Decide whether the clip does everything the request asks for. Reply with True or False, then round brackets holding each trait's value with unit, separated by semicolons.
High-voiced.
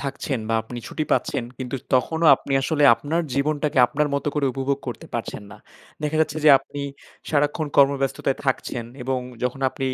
False (140 Hz)